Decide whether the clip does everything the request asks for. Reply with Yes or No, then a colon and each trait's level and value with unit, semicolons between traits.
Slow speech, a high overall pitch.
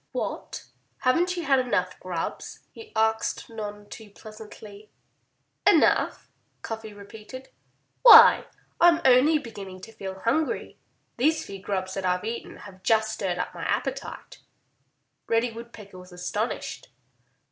Yes: slow, 125 wpm; high, 220 Hz